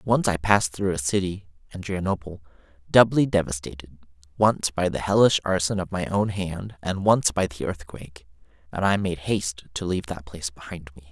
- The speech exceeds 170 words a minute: Yes, average, 180 wpm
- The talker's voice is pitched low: Yes, very low, 90 Hz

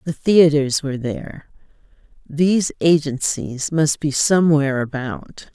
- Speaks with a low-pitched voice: No, medium, 150 Hz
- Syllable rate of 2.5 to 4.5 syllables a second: Yes, 4.3 syllables/s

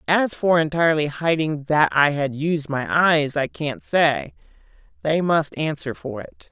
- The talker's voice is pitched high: No, medium, 155 Hz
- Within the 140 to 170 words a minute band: Yes, average, 165 wpm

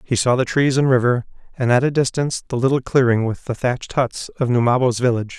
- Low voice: Yes, low, 125 Hz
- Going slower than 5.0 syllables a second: No, 6.3 syllables/s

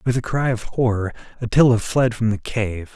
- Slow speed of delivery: No, fast, 205 wpm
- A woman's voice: No, male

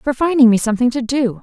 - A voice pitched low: No, very high, 250 Hz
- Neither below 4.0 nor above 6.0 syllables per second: No, 6.5 syllables/s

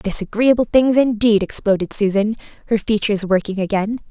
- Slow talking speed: Yes, slow, 130 wpm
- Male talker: No, female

